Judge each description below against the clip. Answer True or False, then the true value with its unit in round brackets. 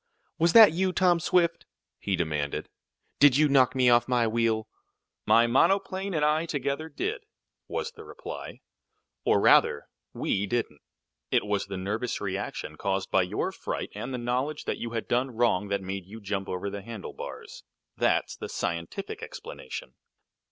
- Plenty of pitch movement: True (6.6 semitones)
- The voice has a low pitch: True (120 Hz)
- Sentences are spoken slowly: False (160 wpm)